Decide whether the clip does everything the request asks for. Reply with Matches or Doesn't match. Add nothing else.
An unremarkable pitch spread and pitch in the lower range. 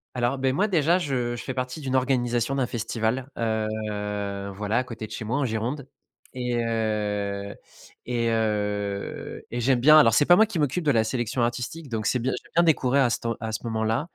Matches